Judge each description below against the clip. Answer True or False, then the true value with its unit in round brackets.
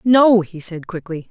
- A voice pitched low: False (185 Hz)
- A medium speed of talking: True (185 wpm)